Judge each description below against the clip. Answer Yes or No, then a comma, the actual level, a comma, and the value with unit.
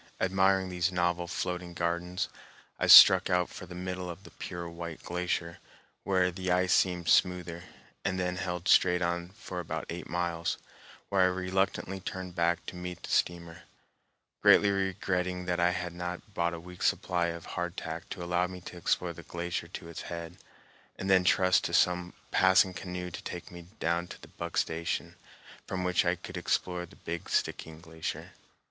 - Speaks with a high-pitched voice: No, very low, 90 Hz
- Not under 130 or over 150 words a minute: No, average, 175 wpm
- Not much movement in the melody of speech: Yes, narrow, 1.1 semitones